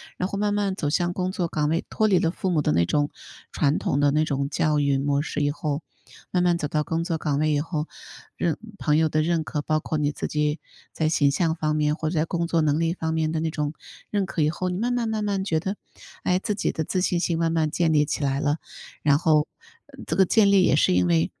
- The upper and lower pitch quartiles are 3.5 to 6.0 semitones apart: No, average, 3.0 semitones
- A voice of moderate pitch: Yes, medium, 160 Hz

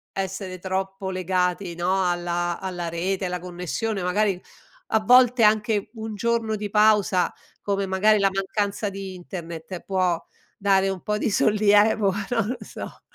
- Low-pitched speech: No, high, 195 Hz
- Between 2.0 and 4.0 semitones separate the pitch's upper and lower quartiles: Yes, narrow, 2.6 semitones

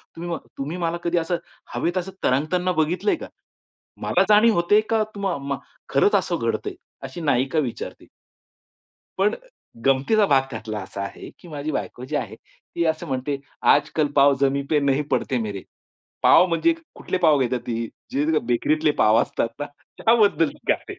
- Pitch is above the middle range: No, medium, 155 Hz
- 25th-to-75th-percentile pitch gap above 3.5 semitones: Yes, average, 5.0 semitones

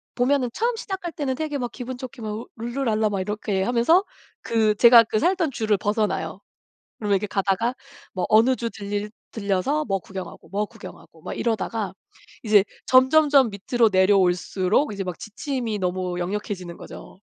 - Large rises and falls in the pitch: No, average, 4.4 semitones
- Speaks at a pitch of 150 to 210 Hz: No, high, 220 Hz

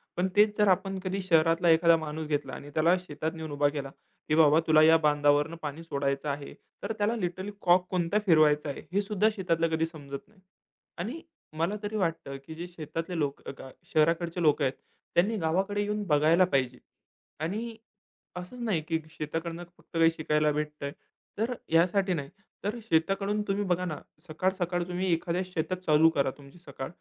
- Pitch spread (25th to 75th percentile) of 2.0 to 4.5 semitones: Yes, average, 3.5 semitones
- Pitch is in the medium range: Yes, medium, 165 Hz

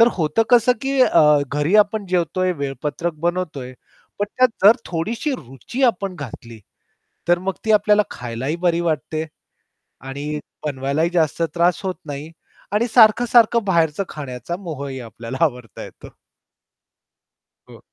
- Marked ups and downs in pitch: Yes, wide, 6.4 semitones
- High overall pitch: No, medium, 170 Hz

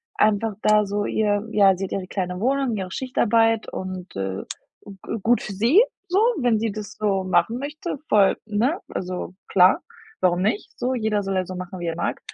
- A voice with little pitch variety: No, average, 3.3 semitones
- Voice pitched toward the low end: No, high, 205 Hz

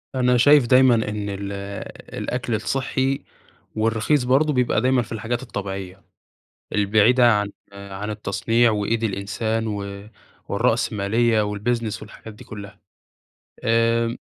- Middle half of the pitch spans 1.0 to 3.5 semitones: Yes, average, 2.9 semitones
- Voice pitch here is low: Yes, low, 110 Hz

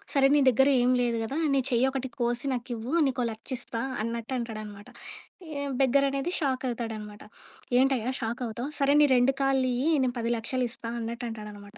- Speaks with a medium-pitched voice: No, high, 245 Hz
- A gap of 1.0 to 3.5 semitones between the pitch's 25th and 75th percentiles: Yes, average, 2.7 semitones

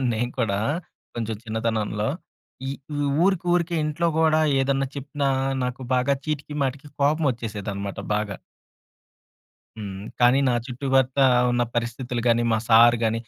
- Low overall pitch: Yes, low, 125 Hz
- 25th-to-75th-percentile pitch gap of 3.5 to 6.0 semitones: Yes, average, 4.0 semitones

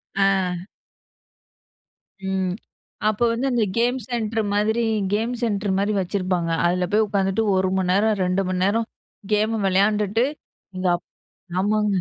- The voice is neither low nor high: No, high, 205 Hz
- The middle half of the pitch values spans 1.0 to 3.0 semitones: Yes, narrow, 2.6 semitones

